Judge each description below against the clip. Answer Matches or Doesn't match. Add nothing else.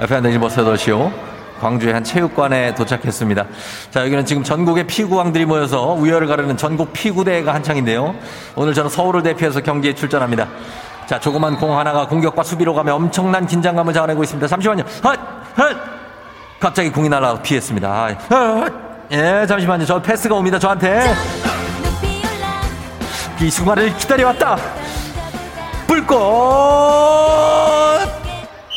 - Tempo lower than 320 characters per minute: Doesn't match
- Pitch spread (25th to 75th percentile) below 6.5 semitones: Doesn't match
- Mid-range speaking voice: Matches